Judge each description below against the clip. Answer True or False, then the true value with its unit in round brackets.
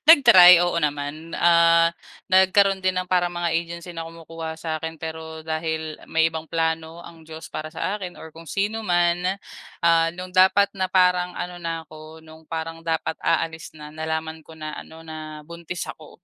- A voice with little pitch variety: True (1.8 semitones)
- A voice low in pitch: False (165 Hz)